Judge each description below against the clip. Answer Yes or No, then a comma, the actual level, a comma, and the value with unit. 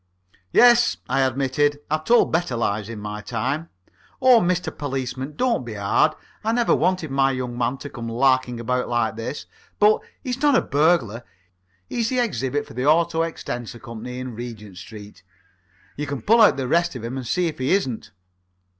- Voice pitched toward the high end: No, low, 135 Hz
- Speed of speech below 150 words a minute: No, average, 180 wpm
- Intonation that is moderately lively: No, wide, 6.2 semitones